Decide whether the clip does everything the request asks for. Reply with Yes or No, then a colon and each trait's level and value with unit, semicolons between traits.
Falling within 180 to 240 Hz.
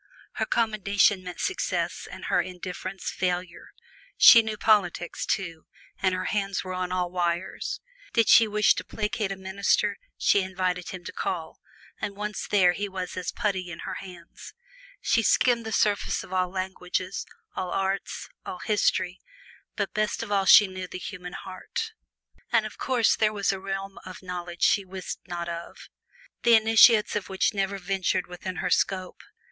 Yes: high, 190 Hz